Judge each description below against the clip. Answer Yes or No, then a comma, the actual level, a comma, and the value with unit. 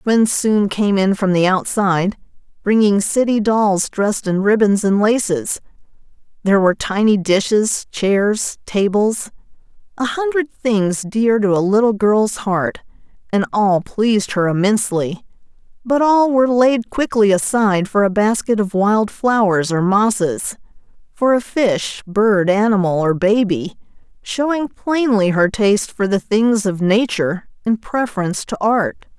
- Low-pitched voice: No, high, 210 Hz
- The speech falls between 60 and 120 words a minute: No, average, 140 wpm